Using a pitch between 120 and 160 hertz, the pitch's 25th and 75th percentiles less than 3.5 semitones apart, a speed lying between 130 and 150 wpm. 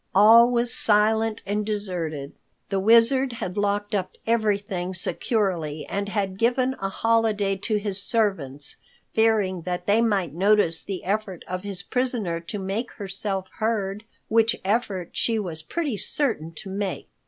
No: high, 205 Hz; average, 3.1 semitones; average, 145 wpm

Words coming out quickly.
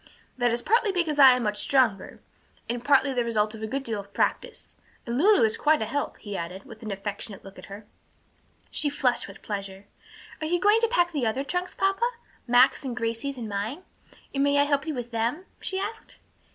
Yes: fast, 215 wpm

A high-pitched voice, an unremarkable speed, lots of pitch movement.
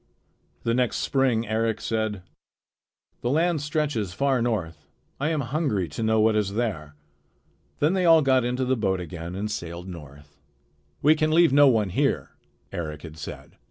No: low, 110 Hz; average, 165 wpm; wide, 7.4 semitones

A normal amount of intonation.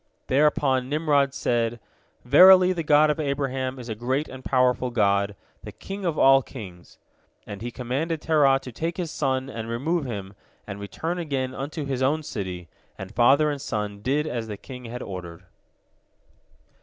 Yes: average, 4.6 semitones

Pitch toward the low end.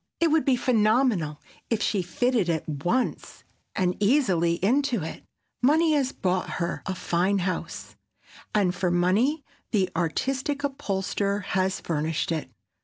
No: high, 200 Hz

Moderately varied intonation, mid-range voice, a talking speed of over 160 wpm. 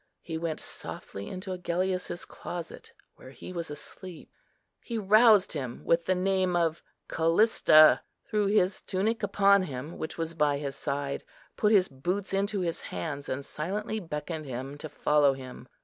No: average, 4.7 semitones; medium, 170 Hz; average, 155 wpm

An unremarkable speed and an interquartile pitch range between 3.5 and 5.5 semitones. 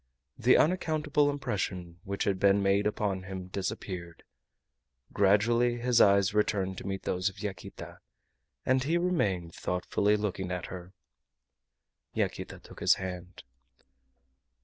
No: slow, 125 wpm; average, 4.1 semitones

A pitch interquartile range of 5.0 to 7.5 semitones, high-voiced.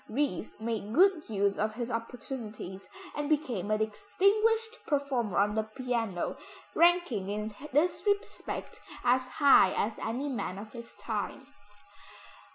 Yes: wide, 5.6 semitones; high, 235 Hz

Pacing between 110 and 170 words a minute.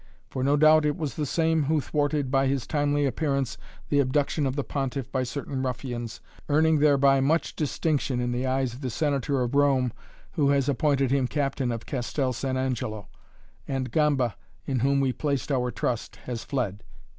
No: average, 180 wpm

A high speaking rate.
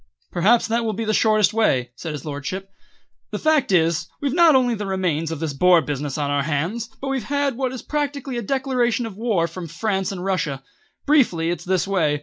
Yes: fast, 210 wpm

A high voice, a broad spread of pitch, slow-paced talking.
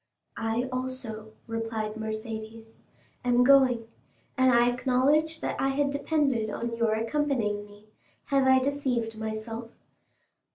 No: high, 235 Hz; average, 3.2 semitones; slow, 115 wpm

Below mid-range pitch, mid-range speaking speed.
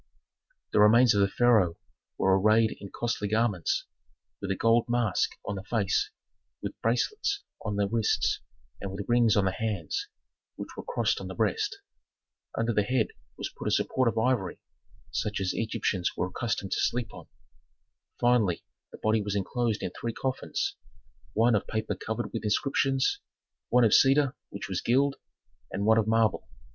Yes: low, 110 Hz; average, 170 wpm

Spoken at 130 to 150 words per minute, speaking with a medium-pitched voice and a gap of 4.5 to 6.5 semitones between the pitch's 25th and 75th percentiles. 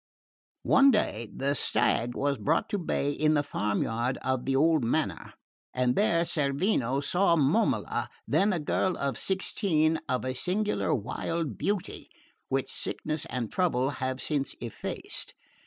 Yes: average, 145 wpm; medium, 145 Hz; average, 5.2 semitones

